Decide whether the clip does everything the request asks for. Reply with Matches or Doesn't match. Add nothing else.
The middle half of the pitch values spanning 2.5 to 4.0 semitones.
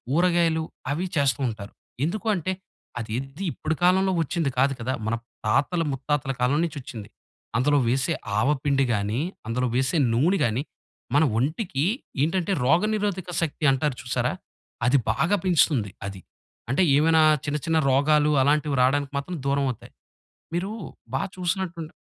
Doesn't match